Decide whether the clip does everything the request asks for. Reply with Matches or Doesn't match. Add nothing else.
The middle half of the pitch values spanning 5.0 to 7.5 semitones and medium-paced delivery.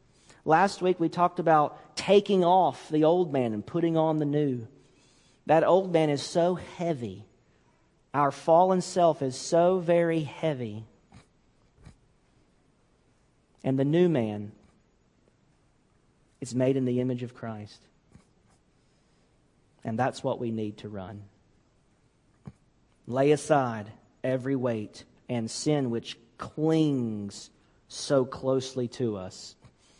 Doesn't match